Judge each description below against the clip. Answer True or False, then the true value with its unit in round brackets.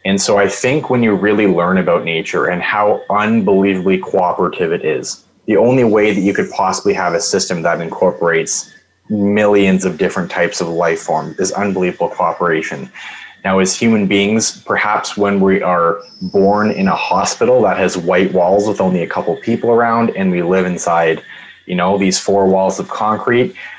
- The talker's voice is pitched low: True (100 Hz)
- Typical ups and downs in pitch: False (2.1 semitones)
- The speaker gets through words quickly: False (180 wpm)